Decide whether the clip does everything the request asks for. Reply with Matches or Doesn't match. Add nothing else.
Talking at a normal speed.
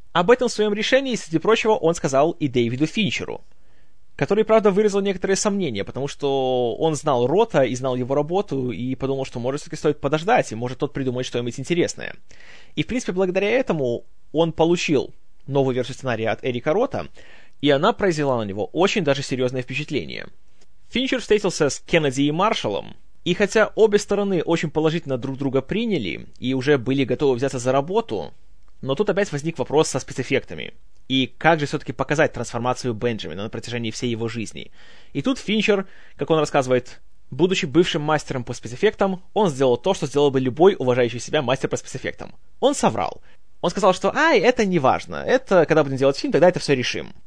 Doesn't match